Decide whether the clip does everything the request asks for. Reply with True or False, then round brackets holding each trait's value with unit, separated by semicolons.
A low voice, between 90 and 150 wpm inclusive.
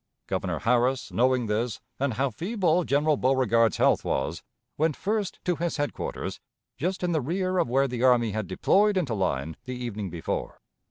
False (130 Hz; 170 wpm)